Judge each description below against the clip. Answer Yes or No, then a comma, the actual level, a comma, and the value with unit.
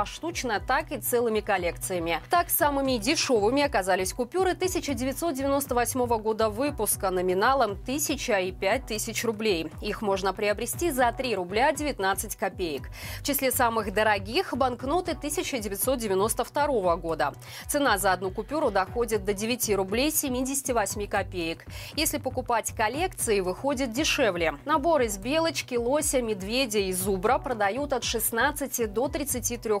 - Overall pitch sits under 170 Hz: No, high, 240 Hz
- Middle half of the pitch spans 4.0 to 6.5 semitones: Yes, wide, 5.6 semitones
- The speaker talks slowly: No, average, 120 wpm